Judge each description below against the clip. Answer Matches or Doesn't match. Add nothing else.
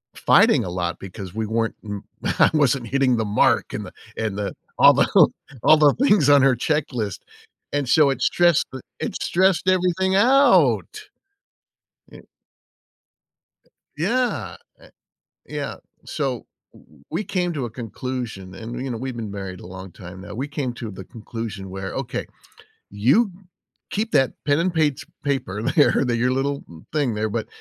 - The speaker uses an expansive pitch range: Matches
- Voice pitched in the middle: Doesn't match